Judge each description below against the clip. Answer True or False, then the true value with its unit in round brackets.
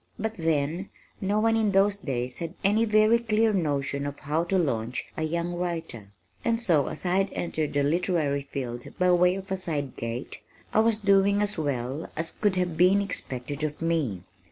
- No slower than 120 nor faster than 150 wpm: False (190 wpm)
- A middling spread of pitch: False (5.7 semitones)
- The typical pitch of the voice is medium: True (170 Hz)